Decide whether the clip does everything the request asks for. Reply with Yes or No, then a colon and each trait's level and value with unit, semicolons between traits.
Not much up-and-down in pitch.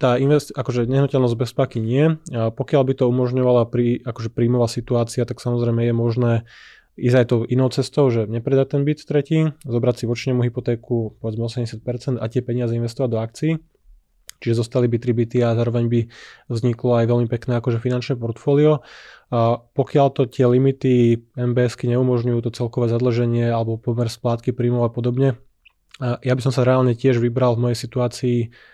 Yes: narrow, 1.5 semitones